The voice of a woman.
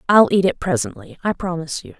Yes: female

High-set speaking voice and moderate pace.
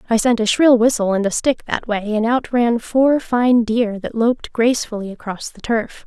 No: high, 230 Hz; fast, 220 wpm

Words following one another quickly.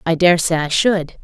Yes: fast, 245 wpm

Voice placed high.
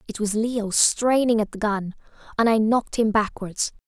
Yes: high, 215 Hz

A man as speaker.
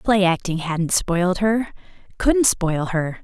No: female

